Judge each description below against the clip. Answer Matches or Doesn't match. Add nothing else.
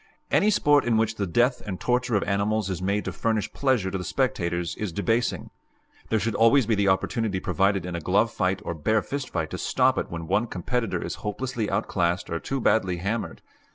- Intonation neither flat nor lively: Matches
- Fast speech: Matches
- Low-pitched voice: Matches